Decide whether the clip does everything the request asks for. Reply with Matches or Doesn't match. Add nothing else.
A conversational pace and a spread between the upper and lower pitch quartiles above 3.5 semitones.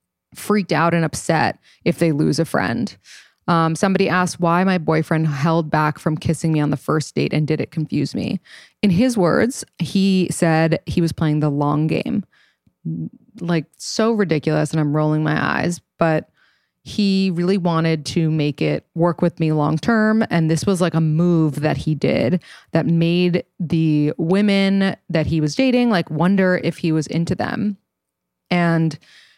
Doesn't match